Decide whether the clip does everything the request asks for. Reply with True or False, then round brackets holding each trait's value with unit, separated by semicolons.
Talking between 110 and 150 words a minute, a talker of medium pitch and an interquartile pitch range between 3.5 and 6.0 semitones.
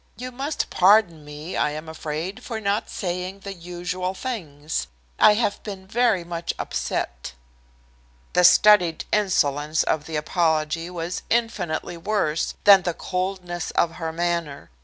True (140 wpm; 175 Hz; 3.8 semitones)